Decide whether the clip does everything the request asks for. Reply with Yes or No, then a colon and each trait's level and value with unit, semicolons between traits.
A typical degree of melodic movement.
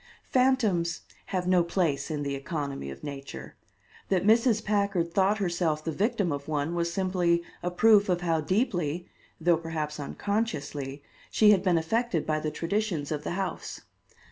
Yes: average, 4.6 semitones